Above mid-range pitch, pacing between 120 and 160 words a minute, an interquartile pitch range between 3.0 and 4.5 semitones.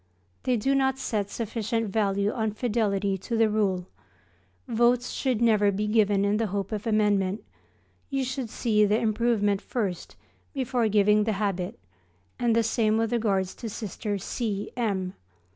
No: high, 215 Hz; average, 155 wpm; narrow, 2.4 semitones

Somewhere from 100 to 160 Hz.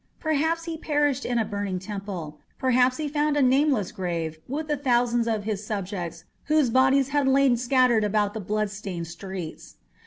No: high, 235 Hz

